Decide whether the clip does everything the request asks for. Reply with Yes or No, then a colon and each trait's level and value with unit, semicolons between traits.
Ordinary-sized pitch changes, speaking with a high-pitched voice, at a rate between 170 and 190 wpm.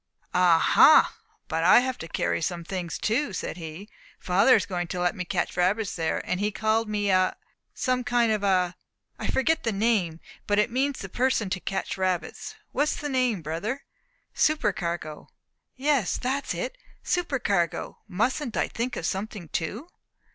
No: wide, 5.9 semitones; high, 205 Hz; average, 175 wpm